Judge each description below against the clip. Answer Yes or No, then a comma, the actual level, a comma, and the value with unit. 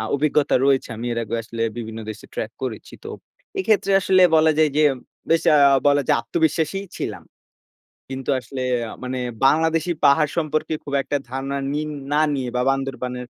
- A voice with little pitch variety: No, average, 3.7 semitones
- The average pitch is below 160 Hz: Yes, medium, 140 Hz